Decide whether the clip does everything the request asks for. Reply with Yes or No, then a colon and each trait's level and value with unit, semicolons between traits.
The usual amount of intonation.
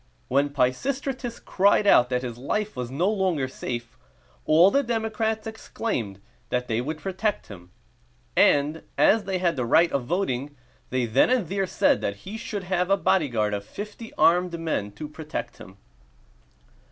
No: wide, 8.4 semitones